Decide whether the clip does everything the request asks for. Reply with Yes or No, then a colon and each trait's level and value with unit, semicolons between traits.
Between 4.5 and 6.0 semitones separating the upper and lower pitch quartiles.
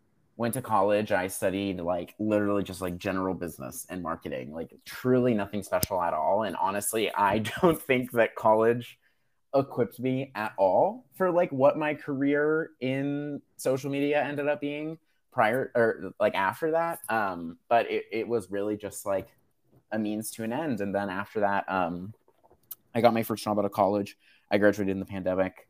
Yes: wide, 5.5 semitones